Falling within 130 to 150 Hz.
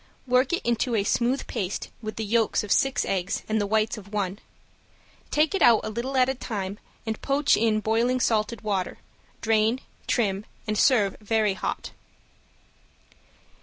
No: high, 220 Hz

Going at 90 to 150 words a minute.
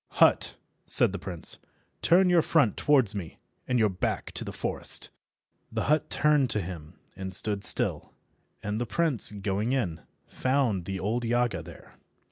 No: average, 160 wpm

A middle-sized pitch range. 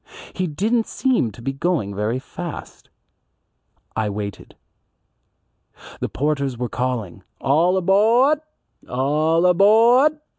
No: wide, 8.4 semitones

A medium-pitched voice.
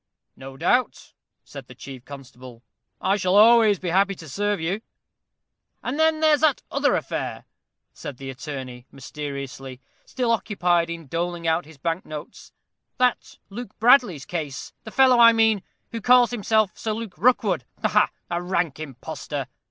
Yes: medium, 180 Hz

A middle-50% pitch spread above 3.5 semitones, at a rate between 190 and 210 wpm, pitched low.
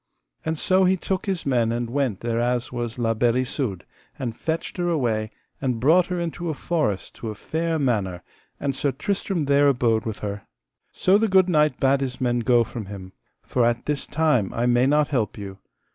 Yes: wide, 5.5 semitones; average, 200 wpm; low, 130 Hz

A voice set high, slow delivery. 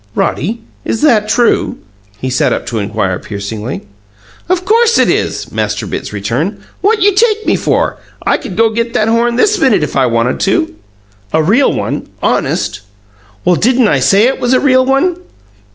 No: high, 230 Hz; average, 180 wpm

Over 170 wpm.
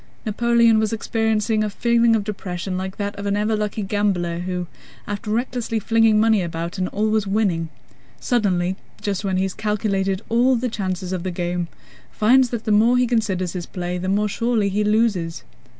Yes: average, 180 wpm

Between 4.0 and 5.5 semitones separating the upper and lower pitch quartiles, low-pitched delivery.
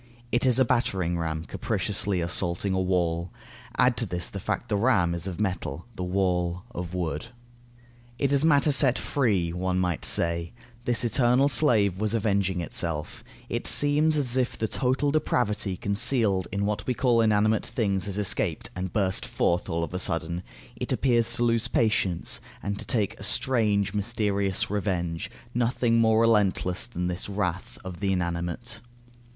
Yes: average, 4.7 semitones; low, 100 Hz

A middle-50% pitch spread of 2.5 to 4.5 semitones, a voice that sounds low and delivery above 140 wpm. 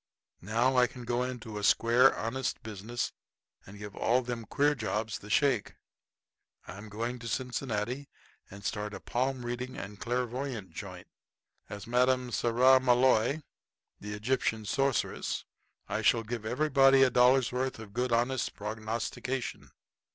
No: average, 2.9 semitones; low, 120 Hz; slow, 135 wpm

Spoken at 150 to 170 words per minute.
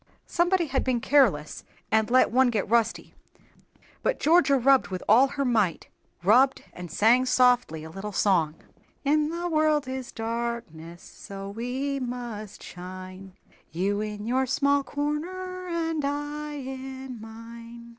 No: slow, 135 wpm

